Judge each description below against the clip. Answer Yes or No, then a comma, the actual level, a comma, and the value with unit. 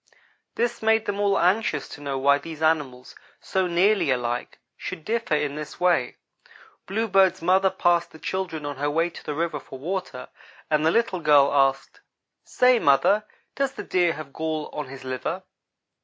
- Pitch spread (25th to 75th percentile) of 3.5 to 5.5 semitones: Yes, average, 5.1 semitones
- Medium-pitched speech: Yes, medium, 160 Hz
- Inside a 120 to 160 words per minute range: No, average, 170 wpm